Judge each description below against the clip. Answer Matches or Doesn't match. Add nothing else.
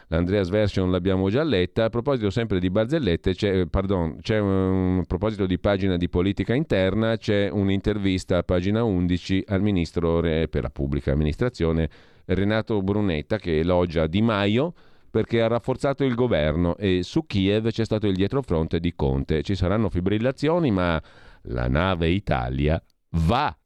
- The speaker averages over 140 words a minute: Matches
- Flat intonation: Doesn't match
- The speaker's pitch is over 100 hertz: Doesn't match